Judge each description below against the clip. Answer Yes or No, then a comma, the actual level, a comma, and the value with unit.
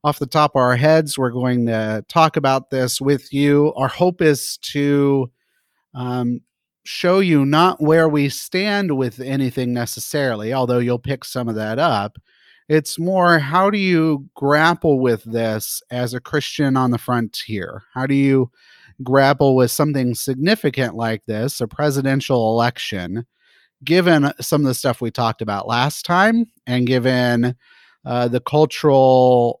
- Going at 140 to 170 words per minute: Yes, average, 155 wpm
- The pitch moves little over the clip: No, average, 3.4 semitones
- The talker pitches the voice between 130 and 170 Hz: Yes, low, 135 Hz